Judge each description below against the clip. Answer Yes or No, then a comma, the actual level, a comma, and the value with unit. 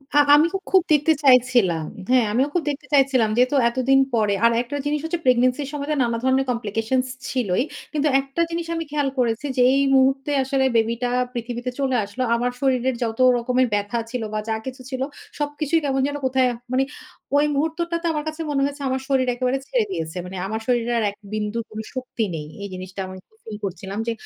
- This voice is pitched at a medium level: No, very high, 255 Hz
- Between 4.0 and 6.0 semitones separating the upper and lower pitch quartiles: No, average, 3.3 semitones